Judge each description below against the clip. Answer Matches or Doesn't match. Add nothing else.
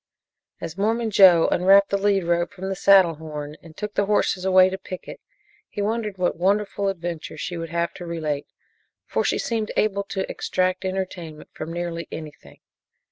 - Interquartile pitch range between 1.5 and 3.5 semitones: Matches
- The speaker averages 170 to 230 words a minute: Matches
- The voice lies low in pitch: Doesn't match